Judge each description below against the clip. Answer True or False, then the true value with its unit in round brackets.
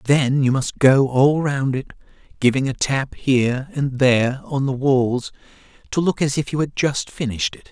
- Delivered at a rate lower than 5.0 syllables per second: True (4.7 syllables/s)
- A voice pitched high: False (135 Hz)